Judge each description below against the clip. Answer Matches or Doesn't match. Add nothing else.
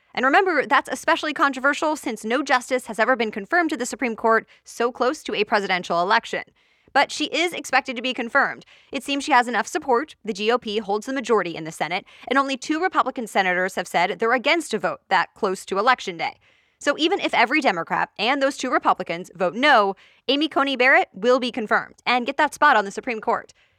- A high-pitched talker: Matches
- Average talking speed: Doesn't match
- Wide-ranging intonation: Doesn't match